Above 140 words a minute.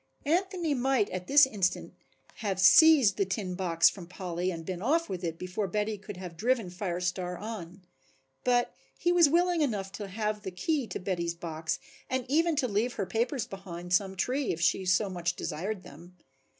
Yes: average, 190 wpm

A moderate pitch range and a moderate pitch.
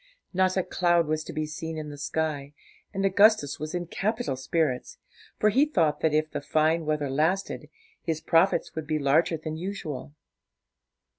Yes: average, 3.0 semitones; medium, 160 Hz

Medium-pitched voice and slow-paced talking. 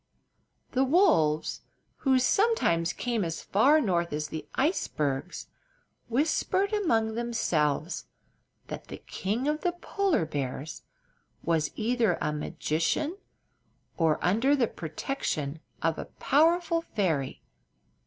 No: high, 220 Hz; slow, 110 wpm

